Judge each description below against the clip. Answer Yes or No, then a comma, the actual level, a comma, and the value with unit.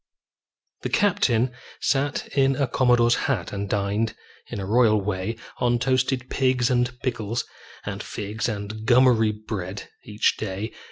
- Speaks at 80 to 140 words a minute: Yes, slow, 135 wpm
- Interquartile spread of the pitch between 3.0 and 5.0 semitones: Yes, average, 3.3 semitones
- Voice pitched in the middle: No, low, 115 Hz